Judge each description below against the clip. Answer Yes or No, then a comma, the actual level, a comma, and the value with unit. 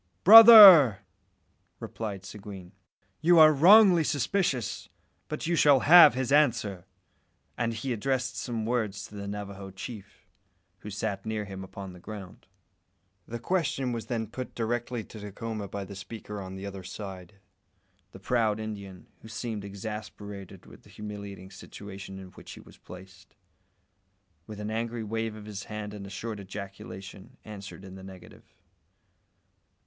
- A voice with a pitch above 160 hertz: No, low, 105 Hz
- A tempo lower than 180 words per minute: Yes, average, 150 wpm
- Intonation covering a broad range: No, average, 3.5 semitones